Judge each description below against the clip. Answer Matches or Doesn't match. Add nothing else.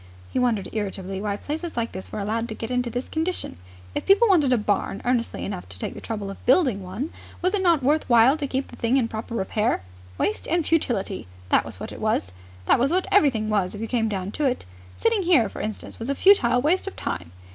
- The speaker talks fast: Matches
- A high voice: Matches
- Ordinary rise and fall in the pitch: Doesn't match